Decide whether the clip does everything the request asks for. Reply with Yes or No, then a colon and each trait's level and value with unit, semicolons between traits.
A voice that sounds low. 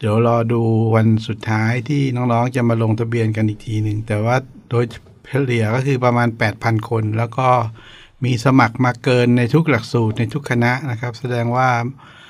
Yes: low, 120 Hz